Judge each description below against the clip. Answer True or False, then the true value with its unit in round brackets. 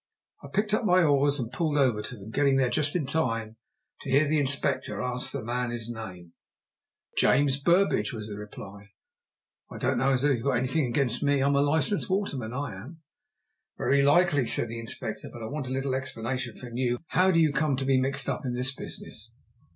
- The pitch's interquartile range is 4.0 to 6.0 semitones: False (3.4 semitones)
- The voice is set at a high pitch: False (135 Hz)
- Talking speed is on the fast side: True (210 wpm)